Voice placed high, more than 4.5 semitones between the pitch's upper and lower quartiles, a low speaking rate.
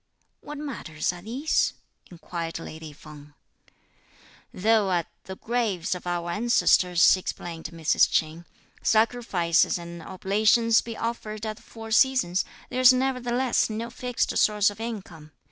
Yes: high, 205 Hz; wide, 5.4 semitones; slow, 130 wpm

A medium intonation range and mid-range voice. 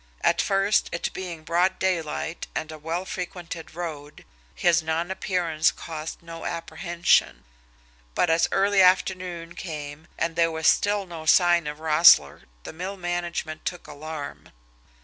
No: narrow, 2.2 semitones; medium, 170 Hz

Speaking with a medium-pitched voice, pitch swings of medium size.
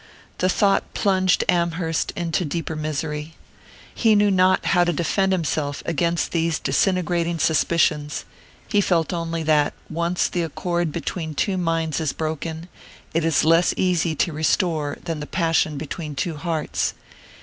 No: medium, 165 Hz; narrow, 2.1 semitones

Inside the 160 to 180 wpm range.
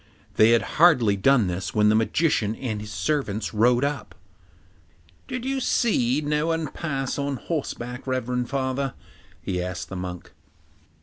No: average, 150 wpm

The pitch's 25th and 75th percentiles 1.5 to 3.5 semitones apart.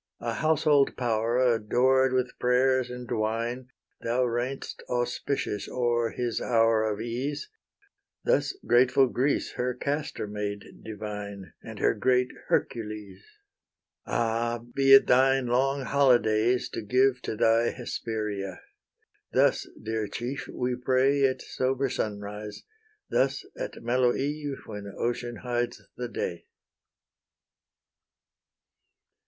Yes: average, 2.7 semitones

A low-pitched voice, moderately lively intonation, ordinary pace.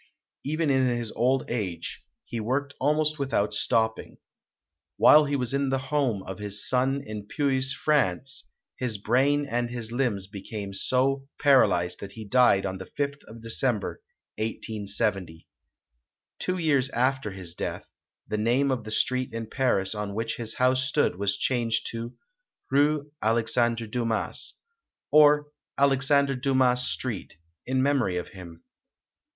Yes: low, 125 Hz; average, 4.3 semitones; average, 145 wpm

